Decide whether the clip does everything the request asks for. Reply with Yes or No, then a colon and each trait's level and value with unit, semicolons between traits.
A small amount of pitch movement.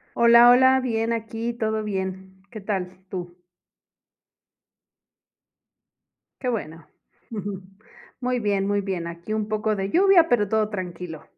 No: average, 3.7 semitones